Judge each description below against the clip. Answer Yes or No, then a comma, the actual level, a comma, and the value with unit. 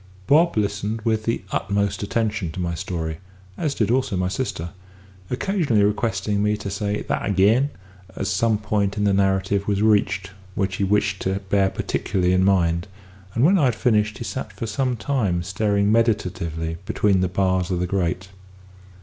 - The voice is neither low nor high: No, low, 100 Hz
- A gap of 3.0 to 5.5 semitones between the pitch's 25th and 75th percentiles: No, narrow, 2.6 semitones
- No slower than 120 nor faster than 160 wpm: No, average, 175 wpm